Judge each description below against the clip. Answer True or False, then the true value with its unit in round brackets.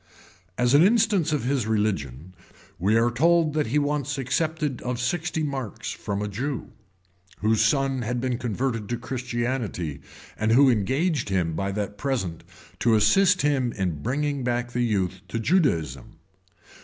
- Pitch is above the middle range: False (120 Hz)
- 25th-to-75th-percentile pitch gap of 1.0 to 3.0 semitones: False (5.4 semitones)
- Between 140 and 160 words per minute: True (155 wpm)